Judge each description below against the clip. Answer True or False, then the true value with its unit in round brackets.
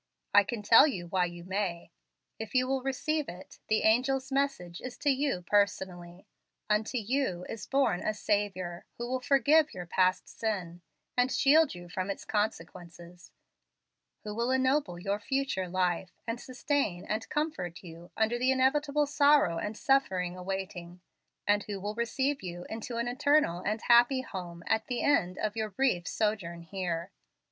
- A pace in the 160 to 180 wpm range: True (165 wpm)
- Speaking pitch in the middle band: False (210 Hz)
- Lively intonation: True (6.4 semitones)